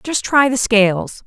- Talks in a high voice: Yes, high, 230 Hz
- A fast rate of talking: No, average, 190 wpm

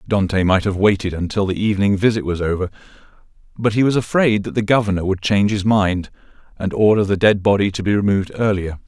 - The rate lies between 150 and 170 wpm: No, fast, 205 wpm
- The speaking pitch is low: Yes, low, 100 Hz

